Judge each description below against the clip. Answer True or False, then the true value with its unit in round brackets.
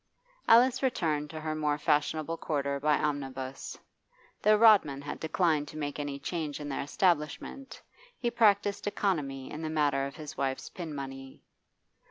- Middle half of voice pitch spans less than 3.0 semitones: False (3.7 semitones)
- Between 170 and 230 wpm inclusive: False (155 wpm)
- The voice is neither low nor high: True (150 Hz)